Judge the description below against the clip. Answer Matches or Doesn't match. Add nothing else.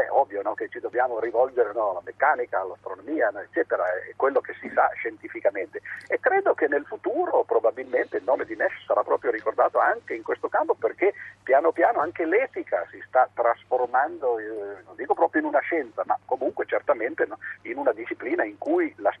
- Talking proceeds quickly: Matches